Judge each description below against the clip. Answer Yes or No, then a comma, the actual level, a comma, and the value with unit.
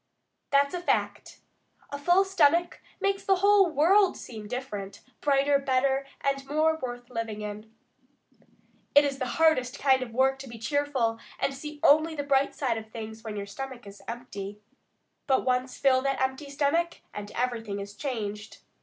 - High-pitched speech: Yes, very high, 265 Hz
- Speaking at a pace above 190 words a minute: No, average, 170 wpm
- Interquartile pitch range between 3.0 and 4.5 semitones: Yes, average, 4.2 semitones